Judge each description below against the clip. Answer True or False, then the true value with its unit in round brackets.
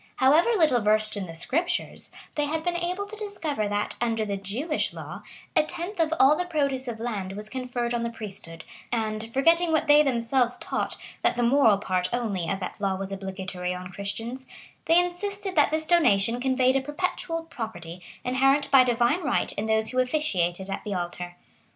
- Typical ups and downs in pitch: False (7.0 semitones)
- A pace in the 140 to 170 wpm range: False (190 wpm)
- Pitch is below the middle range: False (245 Hz)